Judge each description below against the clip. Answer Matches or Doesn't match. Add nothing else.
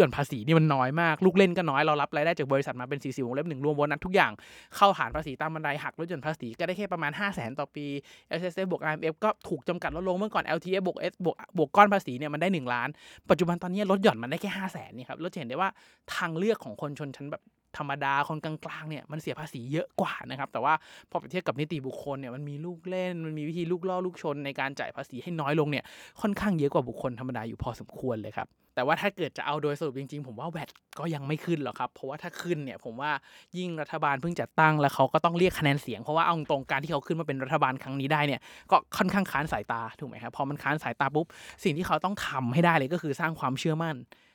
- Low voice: Doesn't match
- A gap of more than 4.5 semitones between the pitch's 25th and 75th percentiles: Doesn't match